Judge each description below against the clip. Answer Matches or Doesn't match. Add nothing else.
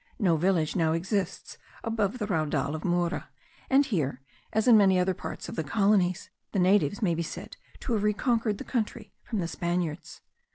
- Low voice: Doesn't match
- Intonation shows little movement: Doesn't match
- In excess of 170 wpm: Matches